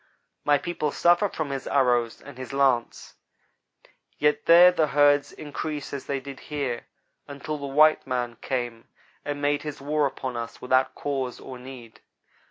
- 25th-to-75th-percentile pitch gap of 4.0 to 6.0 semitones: No, narrow, 2.5 semitones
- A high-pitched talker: No, medium, 140 Hz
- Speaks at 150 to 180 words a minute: Yes, average, 160 wpm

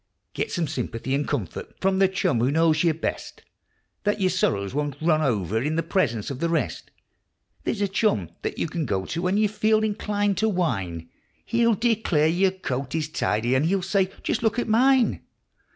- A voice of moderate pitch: Yes, medium, 170 Hz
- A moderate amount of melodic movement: No, wide, 7.0 semitones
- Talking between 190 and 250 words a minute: Yes, average, 195 wpm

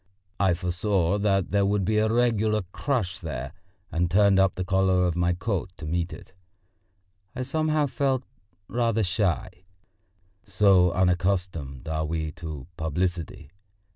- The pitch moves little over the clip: No, average, 3.4 semitones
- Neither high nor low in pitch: No, very low, 95 Hz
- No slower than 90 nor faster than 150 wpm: Yes, average, 140 wpm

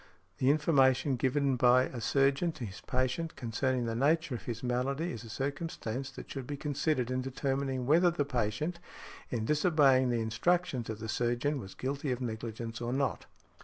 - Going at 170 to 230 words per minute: Yes, average, 175 wpm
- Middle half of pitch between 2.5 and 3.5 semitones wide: Yes, average, 3.1 semitones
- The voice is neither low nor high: No, low, 130 Hz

